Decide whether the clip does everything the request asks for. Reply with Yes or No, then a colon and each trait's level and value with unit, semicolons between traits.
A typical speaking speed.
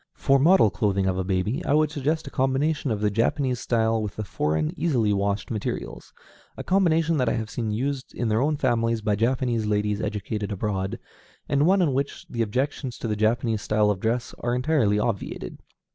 Yes: average, 195 wpm